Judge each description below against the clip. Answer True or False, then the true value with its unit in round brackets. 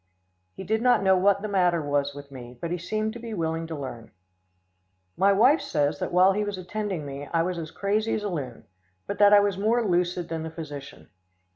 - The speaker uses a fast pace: True (225 wpm)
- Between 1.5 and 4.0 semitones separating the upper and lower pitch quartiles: False (4.9 semitones)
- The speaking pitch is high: False (180 Hz)